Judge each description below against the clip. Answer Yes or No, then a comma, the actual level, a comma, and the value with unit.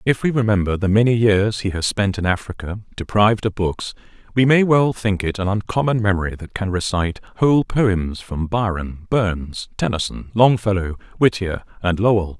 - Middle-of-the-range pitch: No, low, 100 Hz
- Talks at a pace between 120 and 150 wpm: No, average, 170 wpm